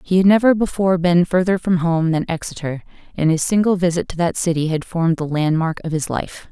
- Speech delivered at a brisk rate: Yes, fast, 220 wpm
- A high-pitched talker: No, medium, 170 Hz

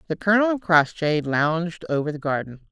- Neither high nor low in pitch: Yes, medium, 165 Hz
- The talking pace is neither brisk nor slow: Yes, average, 175 wpm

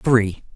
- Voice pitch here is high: No, low, 110 Hz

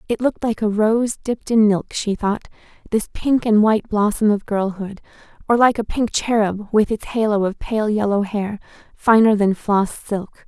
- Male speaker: No, female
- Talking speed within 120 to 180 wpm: No, average, 190 wpm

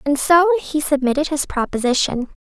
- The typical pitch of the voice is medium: No, very high, 290 Hz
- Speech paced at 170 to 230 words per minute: No, average, 150 wpm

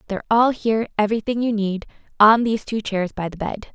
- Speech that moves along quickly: Yes, fast, 210 wpm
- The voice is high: Yes, high, 215 Hz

